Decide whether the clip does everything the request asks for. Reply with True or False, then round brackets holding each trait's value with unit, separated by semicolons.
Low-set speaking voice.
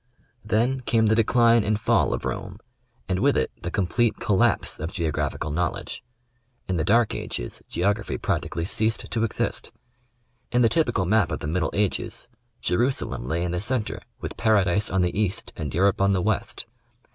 True (100 Hz)